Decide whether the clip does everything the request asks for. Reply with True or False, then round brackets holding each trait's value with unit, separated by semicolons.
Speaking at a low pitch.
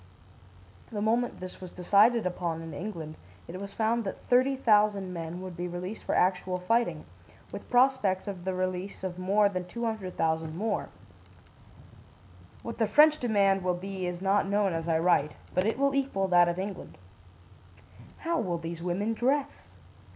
False (190 Hz)